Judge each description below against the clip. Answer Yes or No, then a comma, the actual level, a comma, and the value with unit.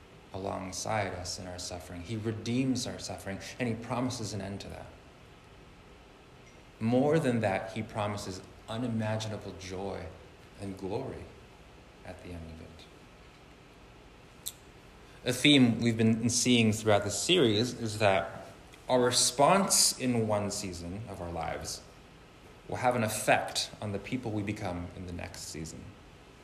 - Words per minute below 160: Yes, average, 140 wpm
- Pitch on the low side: Yes, low, 100 Hz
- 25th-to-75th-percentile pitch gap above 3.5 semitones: Yes, average, 4.1 semitones